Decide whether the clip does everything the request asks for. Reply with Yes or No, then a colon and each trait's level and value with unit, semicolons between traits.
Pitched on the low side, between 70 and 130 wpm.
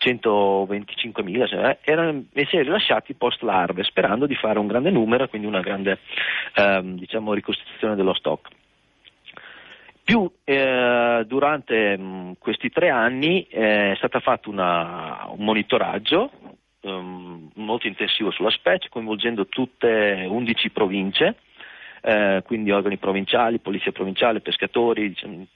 Yes: low, 105 Hz; average, 120 wpm